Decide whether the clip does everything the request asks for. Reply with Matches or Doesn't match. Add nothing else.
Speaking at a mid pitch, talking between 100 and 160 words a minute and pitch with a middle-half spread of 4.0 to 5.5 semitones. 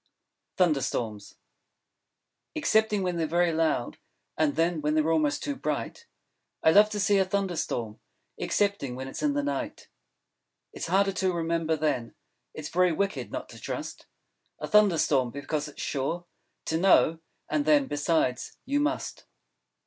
Matches